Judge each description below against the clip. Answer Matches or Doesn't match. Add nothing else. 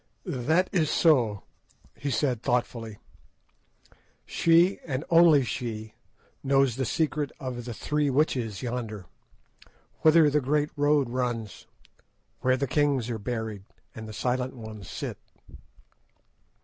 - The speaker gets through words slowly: Matches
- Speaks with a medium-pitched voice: Doesn't match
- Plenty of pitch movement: Doesn't match